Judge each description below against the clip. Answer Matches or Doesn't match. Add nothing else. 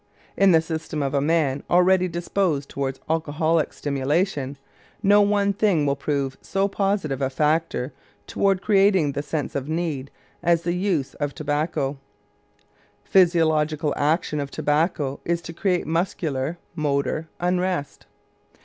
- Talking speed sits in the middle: Doesn't match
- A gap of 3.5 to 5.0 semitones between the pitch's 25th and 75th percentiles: Matches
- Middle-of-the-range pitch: Matches